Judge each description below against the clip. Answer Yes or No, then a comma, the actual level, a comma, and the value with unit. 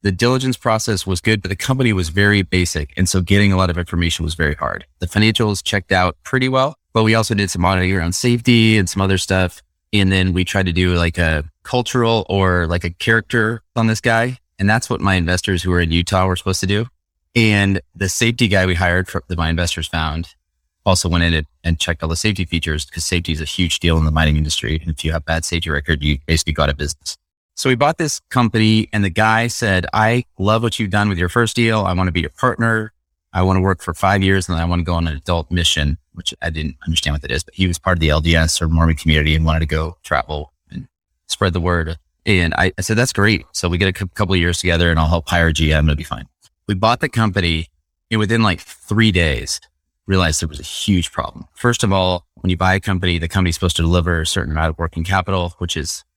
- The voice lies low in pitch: Yes, very low, 90 Hz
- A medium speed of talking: No, fast, 255 wpm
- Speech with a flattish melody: No, average, 4.0 semitones